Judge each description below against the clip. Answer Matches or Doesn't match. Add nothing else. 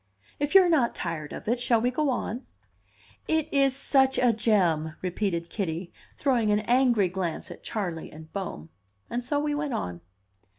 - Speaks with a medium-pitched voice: Doesn't match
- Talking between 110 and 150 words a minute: Doesn't match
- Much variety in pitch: Matches